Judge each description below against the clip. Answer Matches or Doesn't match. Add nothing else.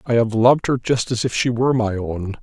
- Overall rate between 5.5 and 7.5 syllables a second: Matches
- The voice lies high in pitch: Doesn't match